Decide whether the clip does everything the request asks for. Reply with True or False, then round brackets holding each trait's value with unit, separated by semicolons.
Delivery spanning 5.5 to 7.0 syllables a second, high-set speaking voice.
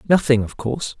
False (6.2 syllables/s; 130 Hz)